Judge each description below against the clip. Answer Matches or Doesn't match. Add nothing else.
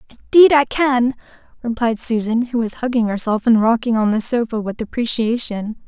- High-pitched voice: Matches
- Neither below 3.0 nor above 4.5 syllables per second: Doesn't match